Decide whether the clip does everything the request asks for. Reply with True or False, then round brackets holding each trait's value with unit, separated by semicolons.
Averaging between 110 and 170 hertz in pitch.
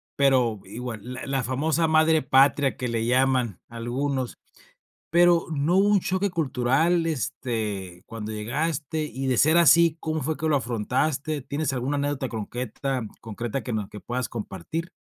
True (135 Hz)